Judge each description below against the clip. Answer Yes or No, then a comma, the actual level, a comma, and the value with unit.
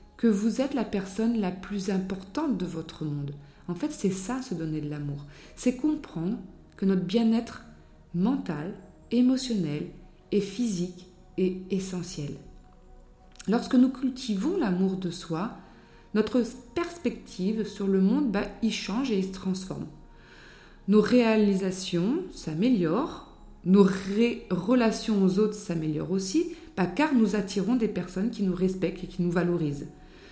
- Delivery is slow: Yes, slow, 140 wpm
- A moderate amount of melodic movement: Yes, average, 4.5 semitones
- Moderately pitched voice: No, high, 195 Hz